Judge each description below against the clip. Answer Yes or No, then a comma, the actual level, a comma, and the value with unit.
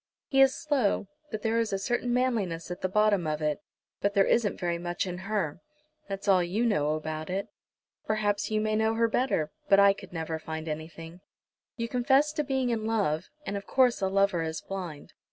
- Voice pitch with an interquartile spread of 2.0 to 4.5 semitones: No, average, 5.0 semitones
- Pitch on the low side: No, high, 200 Hz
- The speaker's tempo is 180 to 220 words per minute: Yes, fast, 205 wpm